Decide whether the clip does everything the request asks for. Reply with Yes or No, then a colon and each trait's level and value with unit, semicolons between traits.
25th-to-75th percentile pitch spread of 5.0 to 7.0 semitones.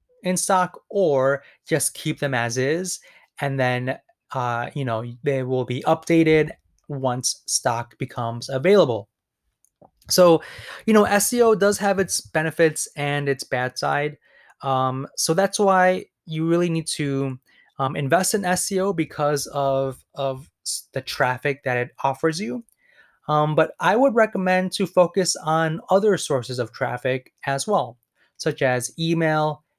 Yes: wide, 5.6 semitones